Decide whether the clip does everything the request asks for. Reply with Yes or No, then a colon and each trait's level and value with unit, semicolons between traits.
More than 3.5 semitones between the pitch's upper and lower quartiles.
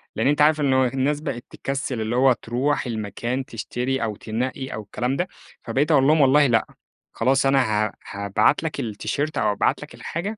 Yes: average, 3.9 semitones